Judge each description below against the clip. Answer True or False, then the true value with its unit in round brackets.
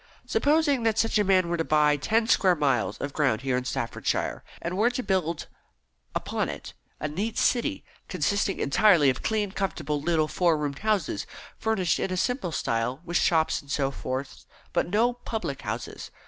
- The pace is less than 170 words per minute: False (175 wpm)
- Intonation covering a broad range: True (7.3 semitones)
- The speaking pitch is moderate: True (170 Hz)